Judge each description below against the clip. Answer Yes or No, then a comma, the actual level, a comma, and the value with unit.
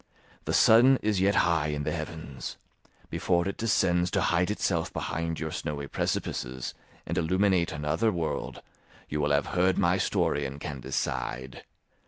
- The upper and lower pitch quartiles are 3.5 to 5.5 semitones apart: Yes, average, 4.1 semitones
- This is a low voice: Yes, very low, 80 Hz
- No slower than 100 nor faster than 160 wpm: Yes, average, 155 wpm